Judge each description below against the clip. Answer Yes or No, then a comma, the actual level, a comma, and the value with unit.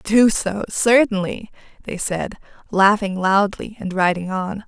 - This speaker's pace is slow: Yes, slow, 130 wpm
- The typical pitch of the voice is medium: No, high, 200 Hz